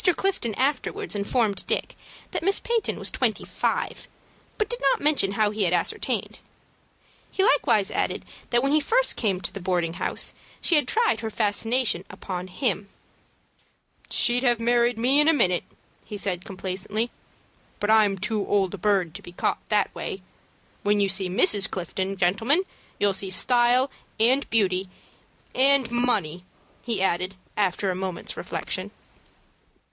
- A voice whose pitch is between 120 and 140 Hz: No, high, 210 Hz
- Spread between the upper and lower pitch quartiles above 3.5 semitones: Yes, average, 4.7 semitones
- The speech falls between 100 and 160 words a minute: Yes, average, 155 wpm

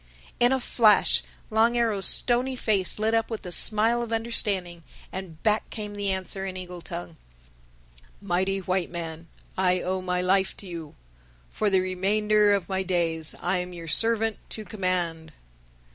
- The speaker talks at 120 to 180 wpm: Yes, average, 160 wpm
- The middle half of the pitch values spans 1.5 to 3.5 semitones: Yes, average, 3.2 semitones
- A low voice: No, high, 190 Hz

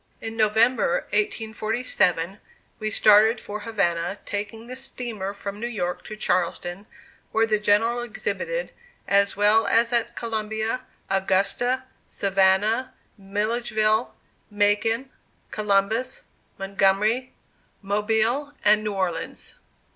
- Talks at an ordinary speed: No, slow, 100 wpm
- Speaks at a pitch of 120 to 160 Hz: No, high, 215 Hz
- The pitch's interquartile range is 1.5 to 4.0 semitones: Yes, narrow, 2.5 semitones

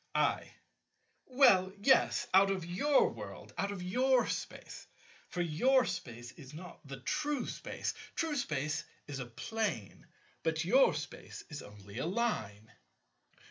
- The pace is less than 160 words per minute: Yes, average, 140 wpm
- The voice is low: No, medium, 185 Hz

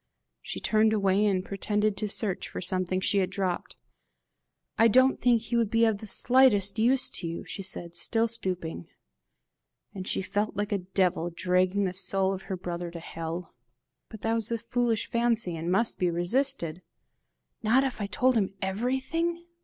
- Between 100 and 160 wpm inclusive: No, average, 175 wpm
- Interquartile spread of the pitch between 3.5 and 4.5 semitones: Yes, average, 3.8 semitones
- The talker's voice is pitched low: No, high, 200 Hz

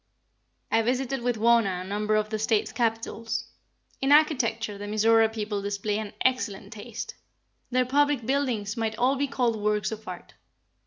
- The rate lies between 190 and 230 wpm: No, average, 160 wpm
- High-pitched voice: Yes, high, 225 Hz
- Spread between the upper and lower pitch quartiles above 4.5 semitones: No, average, 2.9 semitones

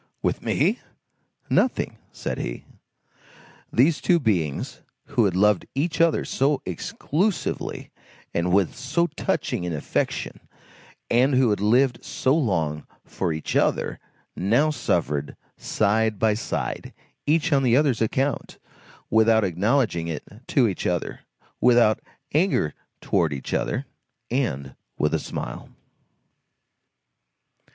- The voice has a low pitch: Yes, low, 110 Hz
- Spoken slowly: Yes, slow, 120 wpm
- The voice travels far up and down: Yes, wide, 7.5 semitones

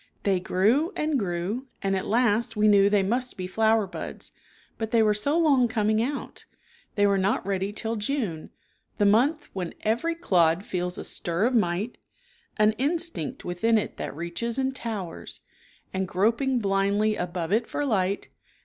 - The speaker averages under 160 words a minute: No, average, 170 wpm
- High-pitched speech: Yes, high, 215 Hz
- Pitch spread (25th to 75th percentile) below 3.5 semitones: No, average, 4.1 semitones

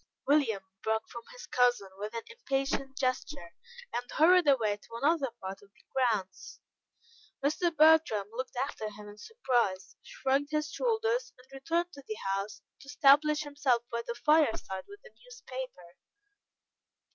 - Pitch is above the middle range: Yes, very high, 265 Hz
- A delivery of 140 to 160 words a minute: Yes, average, 145 wpm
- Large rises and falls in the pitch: Yes, wide, 5.8 semitones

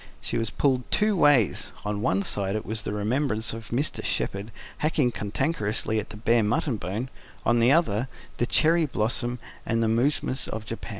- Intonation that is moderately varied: Yes, average, 3.8 semitones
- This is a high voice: No, low, 115 Hz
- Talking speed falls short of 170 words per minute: No, average, 180 wpm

